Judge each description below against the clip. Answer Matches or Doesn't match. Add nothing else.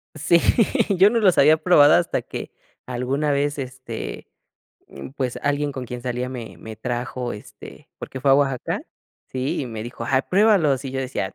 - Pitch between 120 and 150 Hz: Matches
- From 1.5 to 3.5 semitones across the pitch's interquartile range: Matches